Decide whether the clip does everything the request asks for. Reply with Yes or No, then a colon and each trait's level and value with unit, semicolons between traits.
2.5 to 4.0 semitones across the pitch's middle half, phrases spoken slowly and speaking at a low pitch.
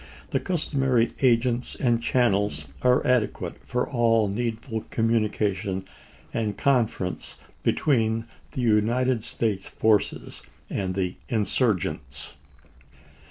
Yes: average, 2.9 semitones; slow, 100 wpm; low, 115 Hz